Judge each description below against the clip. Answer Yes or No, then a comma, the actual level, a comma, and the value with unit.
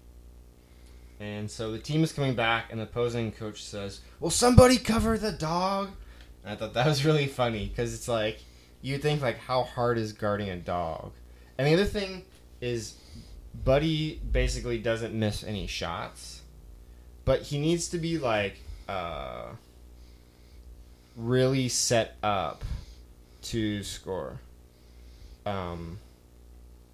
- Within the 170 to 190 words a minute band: No, slow, 135 wpm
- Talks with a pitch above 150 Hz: No, low, 105 Hz